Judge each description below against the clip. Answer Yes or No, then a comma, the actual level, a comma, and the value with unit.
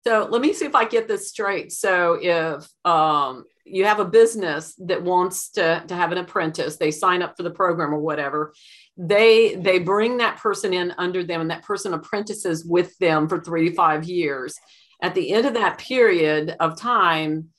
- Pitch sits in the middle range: Yes, medium, 180 Hz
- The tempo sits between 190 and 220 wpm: Yes, average, 200 wpm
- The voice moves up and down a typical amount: Yes, average, 4.3 semitones